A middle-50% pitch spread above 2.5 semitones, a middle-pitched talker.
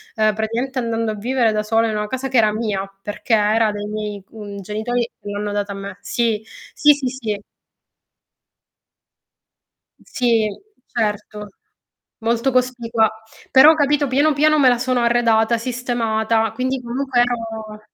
No: average, 2.9 semitones; high, 230 Hz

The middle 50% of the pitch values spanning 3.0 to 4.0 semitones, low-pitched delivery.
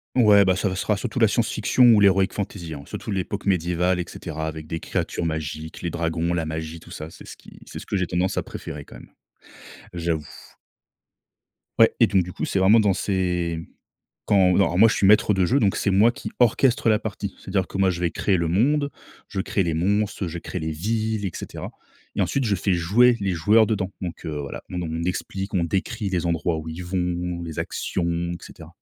Yes: average, 3.4 semitones; very low, 95 Hz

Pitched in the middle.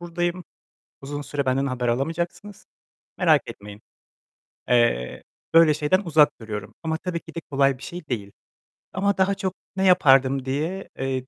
Yes: medium, 145 Hz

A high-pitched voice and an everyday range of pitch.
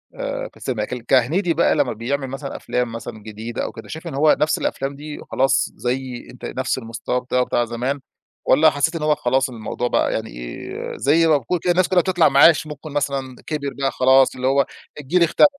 No: low, 135 Hz; average, 3.7 semitones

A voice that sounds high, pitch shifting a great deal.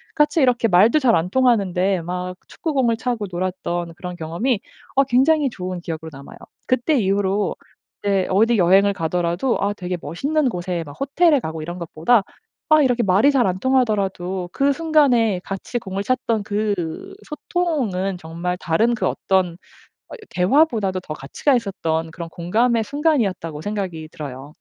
Yes: high, 195 Hz; wide, 5.9 semitones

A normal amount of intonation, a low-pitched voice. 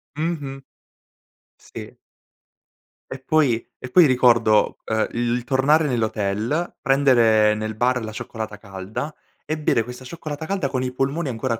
Yes: average, 4.4 semitones; low, 125 Hz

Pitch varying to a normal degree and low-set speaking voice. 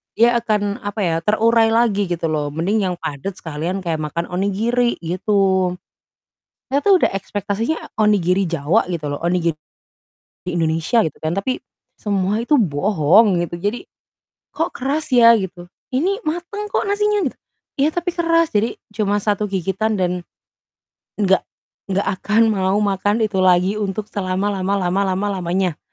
No: average, 4.0 semitones; high, 200 Hz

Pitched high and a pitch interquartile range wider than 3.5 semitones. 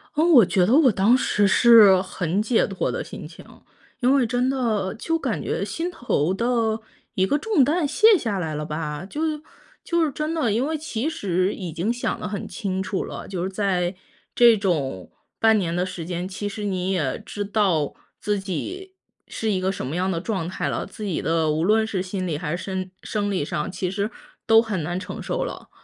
Yes: high, 200 Hz; average, 4.7 semitones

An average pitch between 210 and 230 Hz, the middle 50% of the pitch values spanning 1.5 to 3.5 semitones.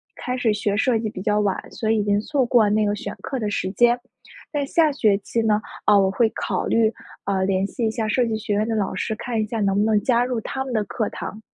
Yes: high, 215 Hz; narrow, 2.5 semitones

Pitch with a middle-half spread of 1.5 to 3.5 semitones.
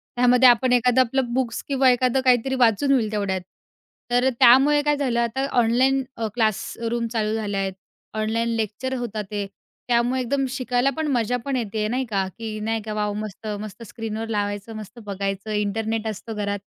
Yes: average, 2.9 semitones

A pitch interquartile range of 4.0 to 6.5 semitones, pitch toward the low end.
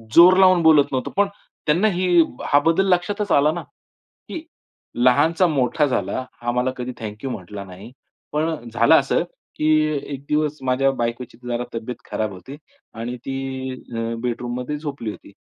Yes: average, 4.7 semitones; low, 130 Hz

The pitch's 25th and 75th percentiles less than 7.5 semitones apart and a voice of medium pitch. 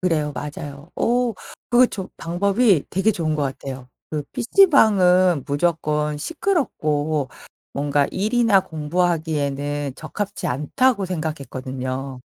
Yes: wide, 5.5 semitones; medium, 160 Hz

